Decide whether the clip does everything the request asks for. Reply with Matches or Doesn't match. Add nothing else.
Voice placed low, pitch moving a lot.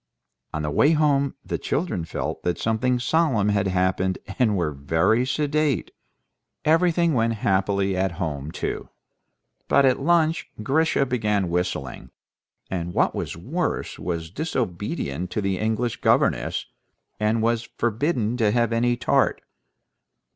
Matches